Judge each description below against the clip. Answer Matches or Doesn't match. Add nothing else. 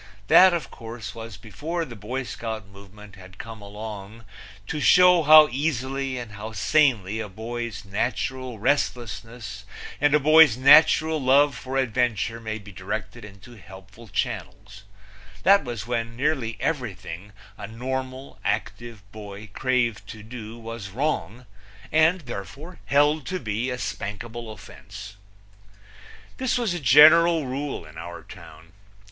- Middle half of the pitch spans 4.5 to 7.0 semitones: Matches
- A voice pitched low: Matches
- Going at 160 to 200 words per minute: Doesn't match